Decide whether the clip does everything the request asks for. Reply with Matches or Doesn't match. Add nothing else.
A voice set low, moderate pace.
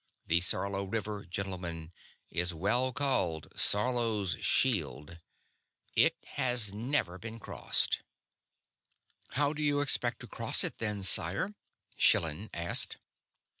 Doesn't match